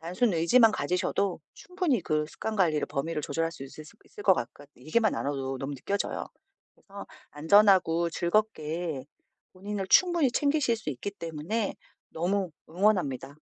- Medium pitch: Yes, medium, 175 Hz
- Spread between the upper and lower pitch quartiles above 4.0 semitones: Yes, wide, 5.5 semitones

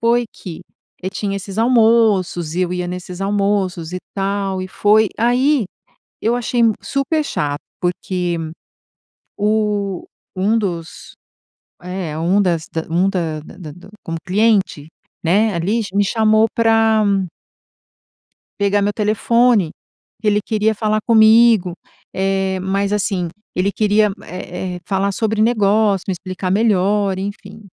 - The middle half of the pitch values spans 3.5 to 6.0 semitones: No, average, 3.0 semitones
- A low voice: No, high, 200 Hz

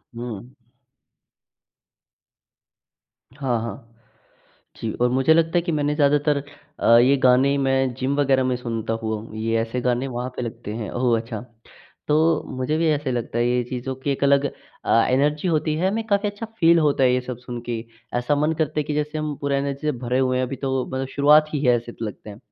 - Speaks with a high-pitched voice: No, low, 130 Hz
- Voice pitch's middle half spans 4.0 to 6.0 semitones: No, average, 3.4 semitones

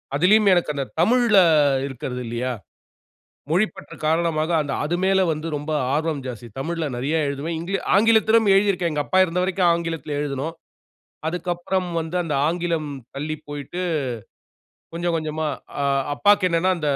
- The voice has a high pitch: No, medium, 165 Hz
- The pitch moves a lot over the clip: No, average, 3.6 semitones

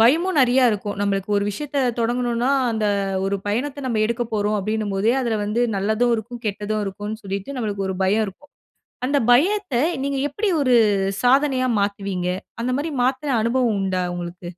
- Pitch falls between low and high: No, high, 225 Hz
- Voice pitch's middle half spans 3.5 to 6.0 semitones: Yes, average, 4.2 semitones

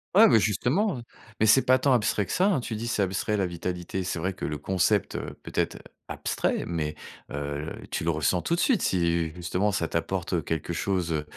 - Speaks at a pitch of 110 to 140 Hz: No, very low, 95 Hz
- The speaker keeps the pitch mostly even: No, average, 4.8 semitones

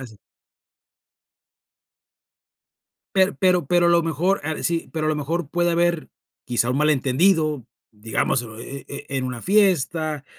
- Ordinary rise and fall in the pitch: Yes, average, 4.2 semitones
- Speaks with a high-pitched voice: No, medium, 155 Hz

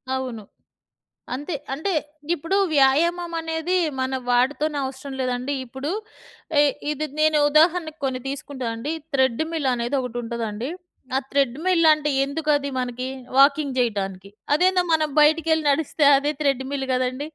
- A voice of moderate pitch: No, very high, 280 Hz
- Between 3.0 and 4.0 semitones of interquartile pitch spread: Yes, average, 3.6 semitones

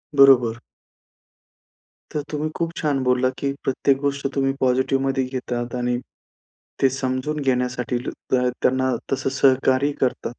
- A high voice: No, low, 130 Hz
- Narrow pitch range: Yes, narrow, 1.4 semitones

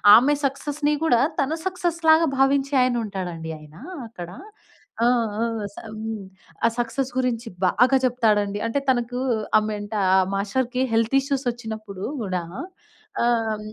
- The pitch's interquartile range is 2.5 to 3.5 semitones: No, average, 4.3 semitones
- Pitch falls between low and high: No, high, 235 Hz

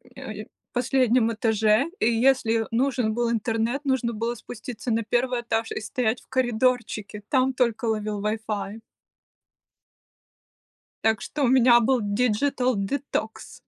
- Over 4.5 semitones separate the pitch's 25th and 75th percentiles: No, narrow, 2.5 semitones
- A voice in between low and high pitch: No, high, 235 Hz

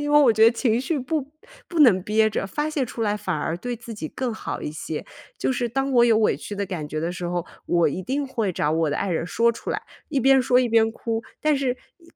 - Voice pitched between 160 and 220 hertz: No, high, 230 Hz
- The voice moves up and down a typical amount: No, wide, 6.0 semitones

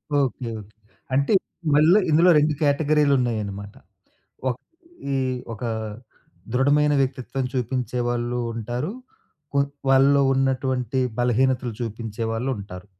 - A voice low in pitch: Yes, low, 130 Hz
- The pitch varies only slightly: No, average, 3.1 semitones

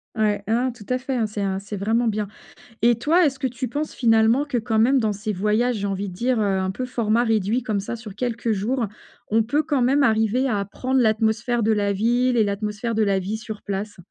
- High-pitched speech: Yes, high, 225 Hz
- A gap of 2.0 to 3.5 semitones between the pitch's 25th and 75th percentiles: Yes, average, 2.9 semitones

